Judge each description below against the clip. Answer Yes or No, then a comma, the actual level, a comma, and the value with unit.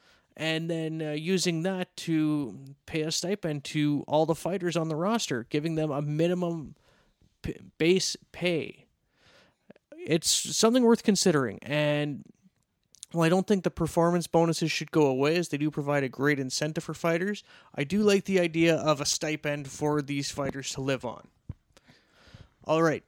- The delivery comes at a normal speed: Yes, average, 165 wpm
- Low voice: No, medium, 160 Hz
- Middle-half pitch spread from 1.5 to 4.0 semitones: Yes, average, 2.9 semitones